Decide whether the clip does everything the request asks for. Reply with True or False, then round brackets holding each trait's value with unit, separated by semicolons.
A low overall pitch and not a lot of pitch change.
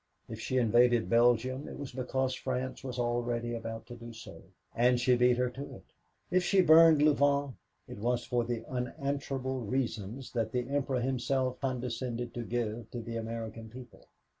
True (125 Hz; 2.0 semitones)